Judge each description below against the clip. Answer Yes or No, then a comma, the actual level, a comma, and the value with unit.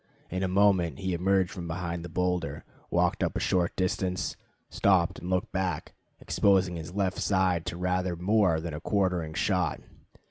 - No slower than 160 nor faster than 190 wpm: Yes, average, 170 wpm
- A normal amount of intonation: No, narrow, 1.7 semitones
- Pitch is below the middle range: Yes, very low, 90 Hz